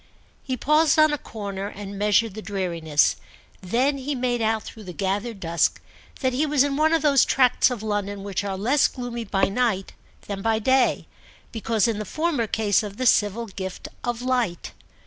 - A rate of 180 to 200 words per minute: Yes, average, 185 wpm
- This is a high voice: Yes, high, 225 Hz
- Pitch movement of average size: Yes, average, 4.3 semitones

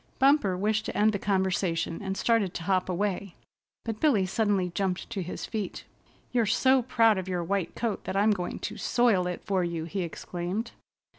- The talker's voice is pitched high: Yes, high, 195 Hz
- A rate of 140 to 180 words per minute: No, average, 190 wpm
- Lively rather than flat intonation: No, average, 3.2 semitones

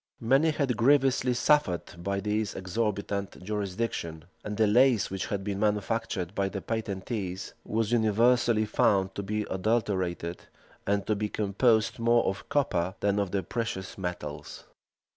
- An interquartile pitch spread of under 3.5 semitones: Yes, average, 3.1 semitones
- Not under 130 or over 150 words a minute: Yes, average, 140 wpm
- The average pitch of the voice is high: No, low, 105 Hz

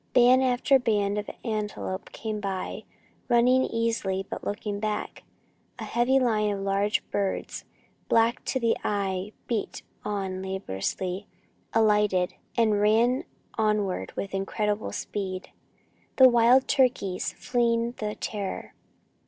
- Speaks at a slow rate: Yes, slow, 120 wpm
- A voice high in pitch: Yes, high, 210 Hz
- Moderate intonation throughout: Yes, average, 3.1 semitones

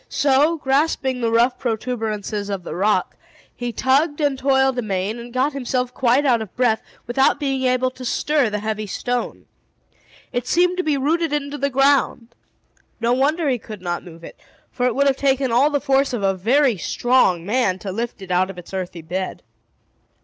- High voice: Yes, very high, 250 Hz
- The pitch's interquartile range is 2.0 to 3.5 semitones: No, average, 4.4 semitones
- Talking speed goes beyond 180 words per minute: Yes, average, 190 wpm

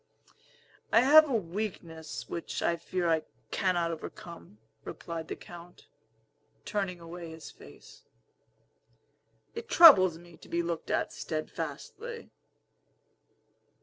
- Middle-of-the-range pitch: Yes, medium, 175 Hz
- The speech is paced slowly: Yes, slow, 110 wpm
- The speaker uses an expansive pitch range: No, average, 3.7 semitones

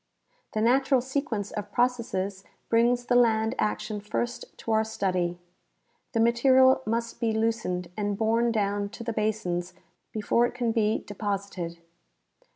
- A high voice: Yes, high, 220 Hz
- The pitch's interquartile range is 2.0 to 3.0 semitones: Yes, average, 2.7 semitones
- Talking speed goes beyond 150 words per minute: No, average, 140 wpm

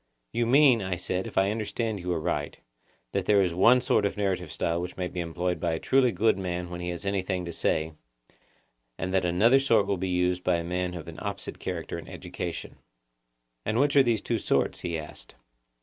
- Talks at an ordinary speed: No, fast, 210 wpm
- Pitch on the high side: No, very low, 95 Hz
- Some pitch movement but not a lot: Yes, average, 3.9 semitones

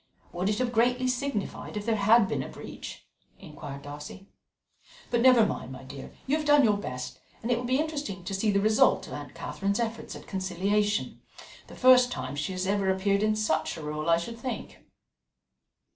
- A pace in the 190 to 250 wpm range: Yes, average, 195 wpm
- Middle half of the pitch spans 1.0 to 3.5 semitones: No, average, 4.7 semitones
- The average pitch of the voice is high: Yes, high, 205 Hz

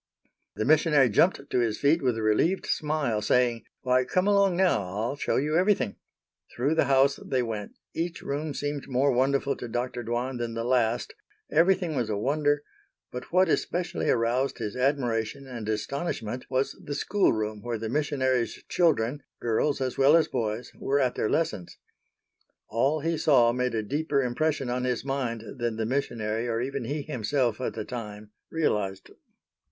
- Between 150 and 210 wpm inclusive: Yes, average, 170 wpm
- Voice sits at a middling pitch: No, low, 130 Hz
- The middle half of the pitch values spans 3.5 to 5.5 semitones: Yes, average, 4.1 semitones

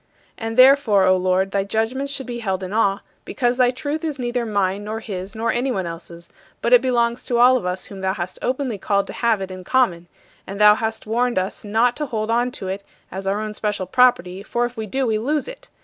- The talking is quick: Yes, fast, 235 wpm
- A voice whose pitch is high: Yes, high, 220 Hz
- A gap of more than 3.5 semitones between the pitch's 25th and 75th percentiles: Yes, average, 4.3 semitones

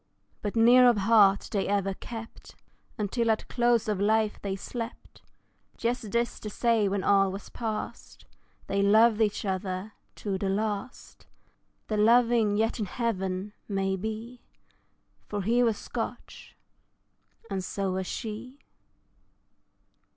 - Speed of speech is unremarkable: No, slow, 130 wpm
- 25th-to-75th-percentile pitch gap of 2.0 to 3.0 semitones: Yes, average, 2.7 semitones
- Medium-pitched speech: No, high, 210 Hz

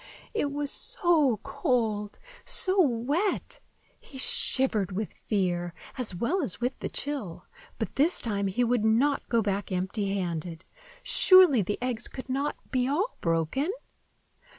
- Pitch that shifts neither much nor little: No, wide, 6.3 semitones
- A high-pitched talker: Yes, high, 240 Hz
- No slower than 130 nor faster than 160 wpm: Yes, average, 140 wpm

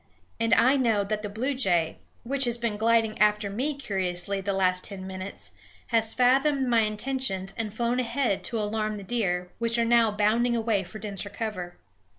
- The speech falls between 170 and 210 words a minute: Yes, average, 175 wpm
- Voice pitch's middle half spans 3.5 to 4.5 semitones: No, average, 3.1 semitones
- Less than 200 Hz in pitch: No, high, 220 Hz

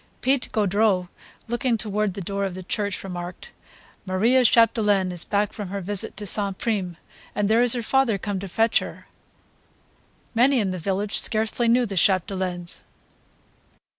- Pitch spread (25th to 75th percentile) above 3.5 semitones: No, average, 3.2 semitones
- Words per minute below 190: Yes, average, 160 wpm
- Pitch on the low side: No, high, 205 Hz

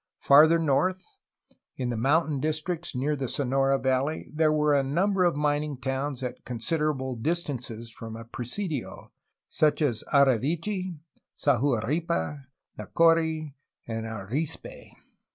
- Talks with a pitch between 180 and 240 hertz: No, medium, 145 Hz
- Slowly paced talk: Yes, slow, 125 wpm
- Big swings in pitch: No, average, 3.8 semitones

